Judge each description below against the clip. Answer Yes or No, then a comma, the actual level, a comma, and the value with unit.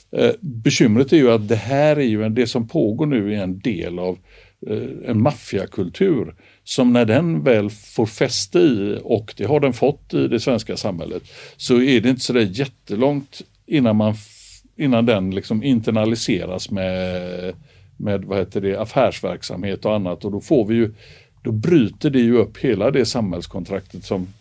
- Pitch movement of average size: Yes, average, 3.8 semitones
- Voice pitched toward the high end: No, low, 110 Hz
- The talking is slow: No, average, 170 wpm